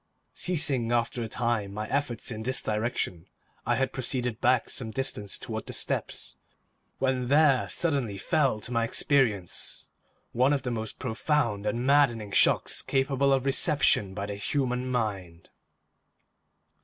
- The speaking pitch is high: No, low, 120 Hz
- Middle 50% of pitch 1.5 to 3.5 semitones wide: No, average, 3.9 semitones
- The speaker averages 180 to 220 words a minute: No, average, 145 wpm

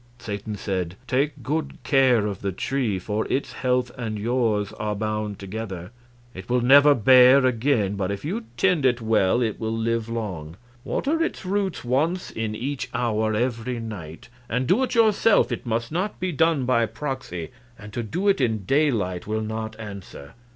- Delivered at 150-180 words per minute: Yes, average, 175 wpm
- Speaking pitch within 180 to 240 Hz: No, low, 115 Hz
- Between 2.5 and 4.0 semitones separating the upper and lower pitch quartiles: No, average, 4.5 semitones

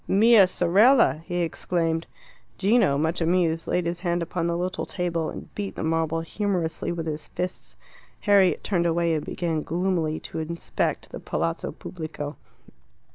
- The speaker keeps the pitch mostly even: Yes, narrow, 2.2 semitones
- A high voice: No, medium, 170 Hz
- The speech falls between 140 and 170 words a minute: Yes, average, 150 wpm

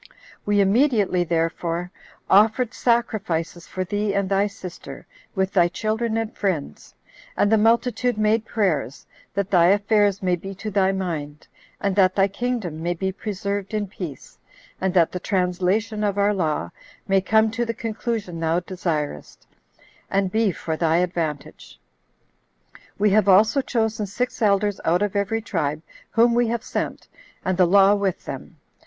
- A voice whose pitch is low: No, high, 195 Hz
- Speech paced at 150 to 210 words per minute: Yes, average, 155 wpm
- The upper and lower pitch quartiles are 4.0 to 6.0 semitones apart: No, average, 3.3 semitones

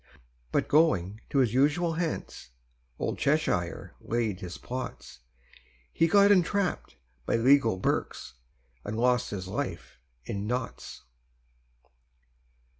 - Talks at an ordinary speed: No, slow, 110 wpm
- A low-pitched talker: Yes, low, 125 Hz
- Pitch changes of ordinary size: No, wide, 7.4 semitones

